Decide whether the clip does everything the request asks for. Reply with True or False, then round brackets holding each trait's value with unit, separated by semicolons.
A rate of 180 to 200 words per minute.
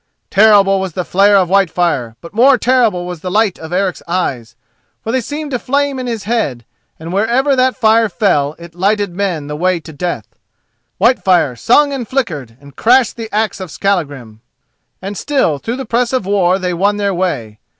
True (190 wpm)